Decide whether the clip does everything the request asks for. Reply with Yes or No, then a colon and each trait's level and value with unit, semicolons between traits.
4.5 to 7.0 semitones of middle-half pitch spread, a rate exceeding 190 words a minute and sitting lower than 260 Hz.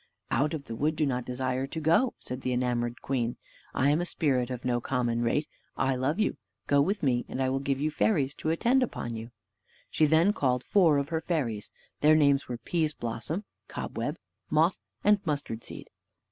No: average, 4.0 semitones; average, 200 wpm; medium, 140 Hz